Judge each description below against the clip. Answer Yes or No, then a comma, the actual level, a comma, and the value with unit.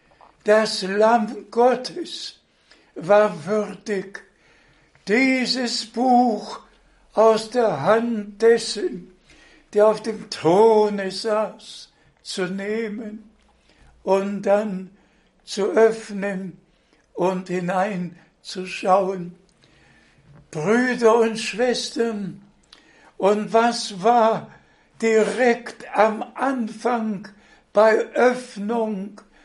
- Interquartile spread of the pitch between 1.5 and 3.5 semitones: Yes, average, 2.9 semitones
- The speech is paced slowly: Yes, slow, 70 wpm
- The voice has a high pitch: Yes, high, 215 Hz